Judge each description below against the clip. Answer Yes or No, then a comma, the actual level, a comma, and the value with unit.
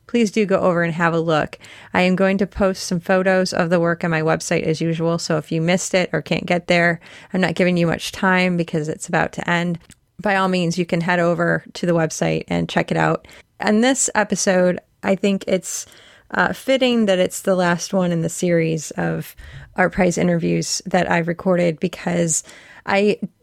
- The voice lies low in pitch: No, medium, 180 Hz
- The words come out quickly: Yes, fast, 210 wpm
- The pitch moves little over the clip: Yes, narrow, 2.2 semitones